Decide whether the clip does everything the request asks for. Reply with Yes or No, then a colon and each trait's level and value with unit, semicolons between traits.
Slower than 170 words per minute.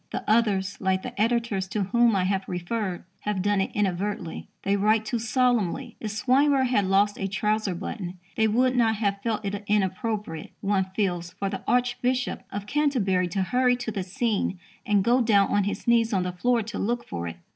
No: average, 195 wpm